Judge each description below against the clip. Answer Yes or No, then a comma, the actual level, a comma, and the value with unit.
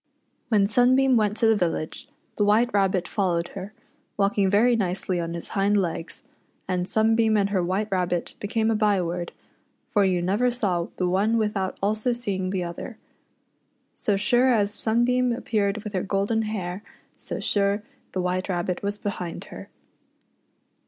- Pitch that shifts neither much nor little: Yes, average, 3.1 semitones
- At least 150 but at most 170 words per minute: Yes, average, 160 wpm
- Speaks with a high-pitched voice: Yes, high, 200 Hz